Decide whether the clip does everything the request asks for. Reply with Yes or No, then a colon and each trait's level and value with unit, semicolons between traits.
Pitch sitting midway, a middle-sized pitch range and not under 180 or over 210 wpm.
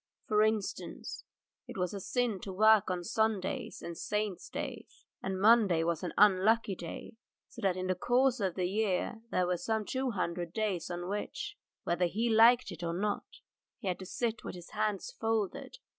No: high, 200 Hz; average, 3.5 semitones; average, 185 wpm